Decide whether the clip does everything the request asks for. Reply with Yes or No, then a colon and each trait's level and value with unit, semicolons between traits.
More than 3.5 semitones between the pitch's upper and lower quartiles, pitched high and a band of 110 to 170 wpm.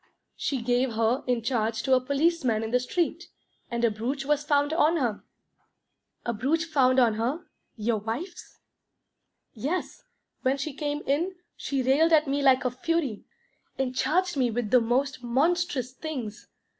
Yes: average, 4.0 semitones; very high, 265 Hz; average, 160 wpm